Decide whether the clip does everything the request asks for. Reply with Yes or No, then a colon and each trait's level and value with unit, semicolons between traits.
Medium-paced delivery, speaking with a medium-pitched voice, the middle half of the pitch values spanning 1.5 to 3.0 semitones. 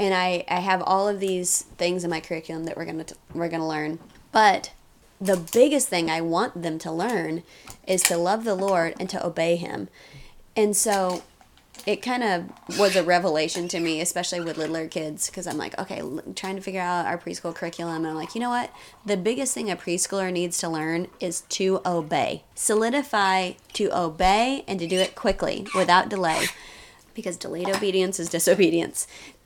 Yes: average, 190 wpm; medium, 180 Hz; narrow, 2.6 semitones